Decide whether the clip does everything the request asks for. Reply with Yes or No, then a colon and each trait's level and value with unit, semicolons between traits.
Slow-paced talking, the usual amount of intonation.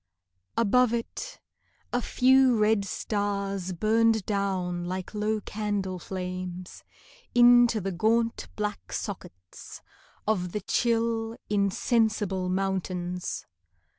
Yes: slow, 95 wpm; average, 3.5 semitones